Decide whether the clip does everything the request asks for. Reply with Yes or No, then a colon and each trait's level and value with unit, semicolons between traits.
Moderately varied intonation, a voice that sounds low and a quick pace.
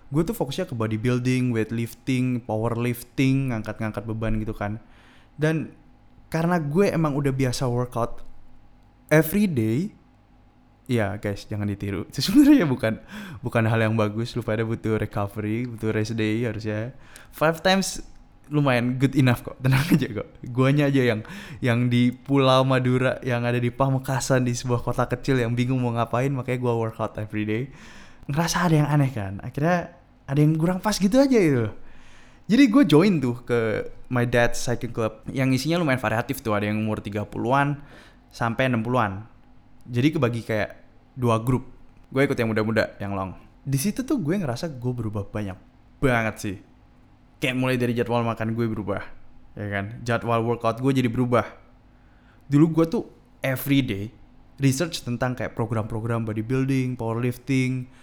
Yes: average, 3.4 semitones; low, 120 Hz; fast, 155 wpm